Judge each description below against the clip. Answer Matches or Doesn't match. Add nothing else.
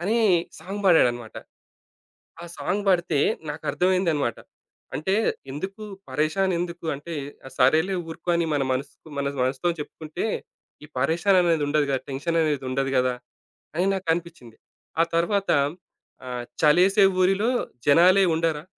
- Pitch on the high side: Doesn't match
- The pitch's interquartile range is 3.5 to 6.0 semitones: Matches